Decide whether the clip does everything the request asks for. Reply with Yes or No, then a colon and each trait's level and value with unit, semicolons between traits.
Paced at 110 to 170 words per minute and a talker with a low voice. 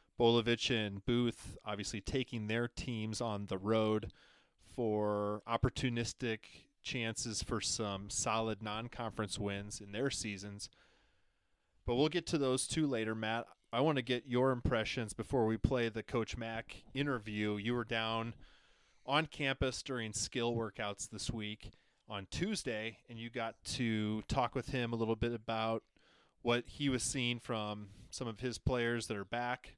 Yes: average, 155 wpm; low, 115 Hz